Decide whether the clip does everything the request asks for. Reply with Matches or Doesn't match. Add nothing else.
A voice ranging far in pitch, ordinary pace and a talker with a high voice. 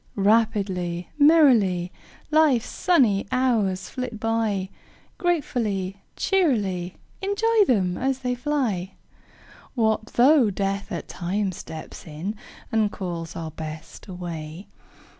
Doesn't match